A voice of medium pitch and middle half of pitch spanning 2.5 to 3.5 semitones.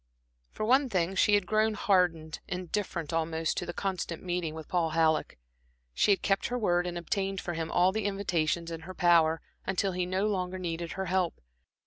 Yes: medium, 180 Hz; average, 2.8 semitones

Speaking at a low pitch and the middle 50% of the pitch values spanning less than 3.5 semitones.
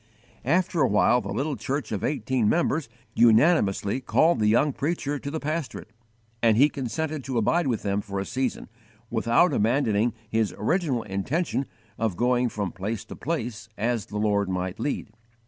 No: low, 120 Hz; wide, 5.5 semitones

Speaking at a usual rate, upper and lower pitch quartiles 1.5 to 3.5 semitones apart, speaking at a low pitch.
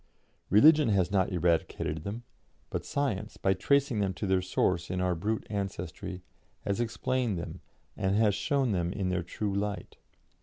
Yes: average, 160 wpm; average, 3.2 semitones; low, 100 Hz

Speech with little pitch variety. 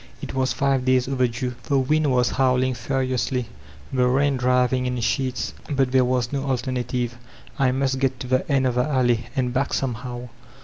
Yes: narrow, 1.2 semitones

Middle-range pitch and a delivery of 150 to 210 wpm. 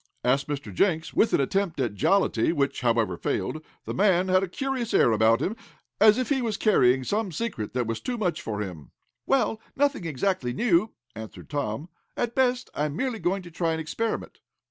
Yes: medium, 170 Hz; average, 195 wpm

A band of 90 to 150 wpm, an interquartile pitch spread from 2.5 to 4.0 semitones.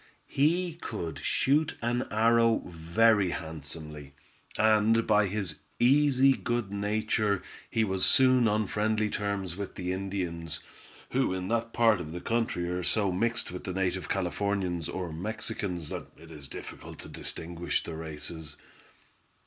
No: average, 140 wpm; average, 4.6 semitones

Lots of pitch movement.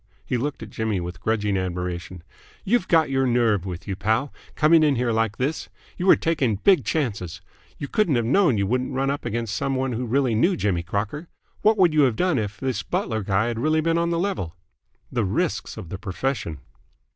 Yes: wide, 6.7 semitones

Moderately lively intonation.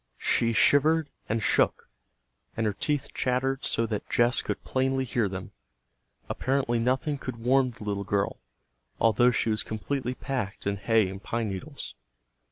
Yes: average, 3.7 semitones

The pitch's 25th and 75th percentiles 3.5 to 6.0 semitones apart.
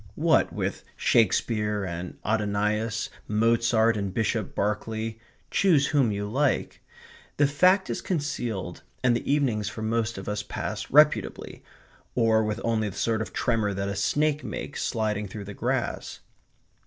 No: narrow, 2.4 semitones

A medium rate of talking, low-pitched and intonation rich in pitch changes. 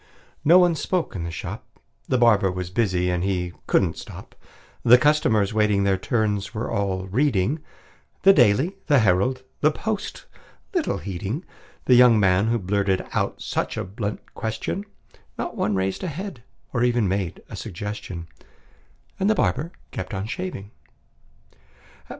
Yes: average, 150 wpm; low, 105 Hz; wide, 6.2 semitones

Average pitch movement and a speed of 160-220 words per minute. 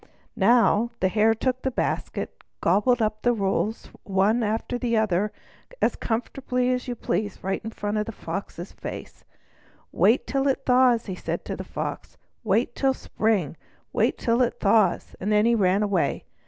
Yes: average, 3.2 semitones; average, 170 wpm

